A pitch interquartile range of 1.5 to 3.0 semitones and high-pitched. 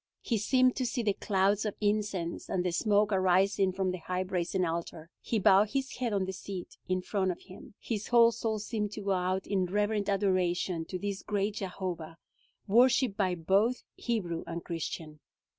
Yes: narrow, 2.6 semitones; high, 195 Hz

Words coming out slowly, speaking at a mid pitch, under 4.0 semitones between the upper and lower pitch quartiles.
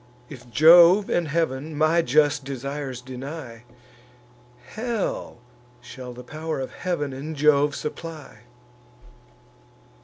Yes: slow, 100 wpm; medium, 145 Hz; average, 3.6 semitones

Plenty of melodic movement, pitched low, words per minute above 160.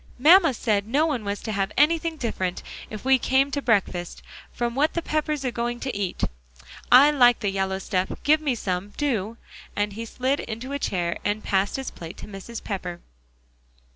No: wide, 5.7 semitones; high, 235 Hz; average, 190 wpm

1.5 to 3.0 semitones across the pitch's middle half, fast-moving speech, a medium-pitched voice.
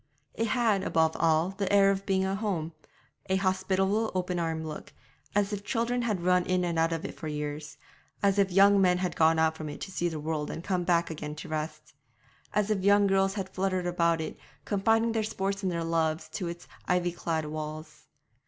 No: average, 3.5 semitones; fast, 210 wpm; medium, 180 Hz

